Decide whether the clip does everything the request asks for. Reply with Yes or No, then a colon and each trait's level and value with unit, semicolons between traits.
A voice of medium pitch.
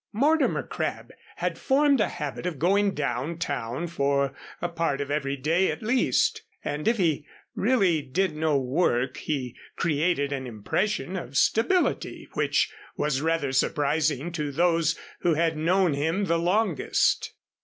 Yes: medium, 160 Hz